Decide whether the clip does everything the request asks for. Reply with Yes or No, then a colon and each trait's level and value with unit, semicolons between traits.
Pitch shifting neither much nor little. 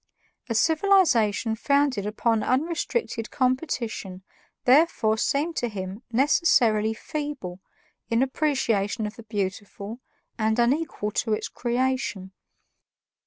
Yes: average, 4.9 semitones